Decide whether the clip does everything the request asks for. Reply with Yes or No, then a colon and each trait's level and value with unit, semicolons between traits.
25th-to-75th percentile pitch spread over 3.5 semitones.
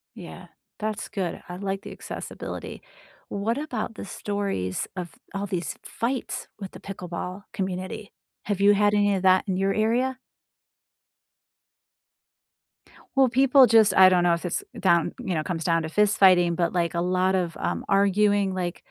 No: average, 2.7 semitones